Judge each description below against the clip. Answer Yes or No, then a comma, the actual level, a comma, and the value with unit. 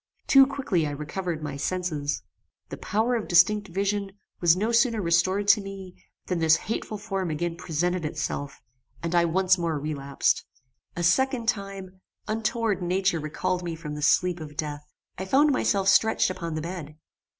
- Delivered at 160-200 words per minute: Yes, average, 165 wpm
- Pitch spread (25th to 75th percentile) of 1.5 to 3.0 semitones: No, average, 3.8 semitones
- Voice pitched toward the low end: No, medium, 180 Hz